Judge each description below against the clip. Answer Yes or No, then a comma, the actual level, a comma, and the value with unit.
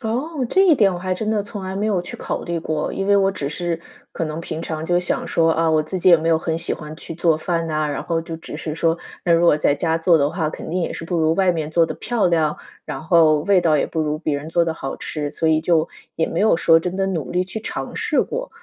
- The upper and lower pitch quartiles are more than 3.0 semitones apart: No, narrow, 2.6 semitones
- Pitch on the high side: No, medium, 165 Hz